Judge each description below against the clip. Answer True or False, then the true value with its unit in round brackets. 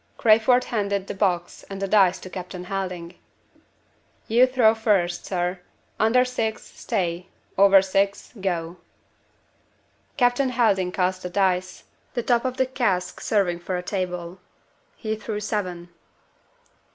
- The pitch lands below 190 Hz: False (195 Hz)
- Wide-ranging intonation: False (3.4 semitones)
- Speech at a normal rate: False (130 wpm)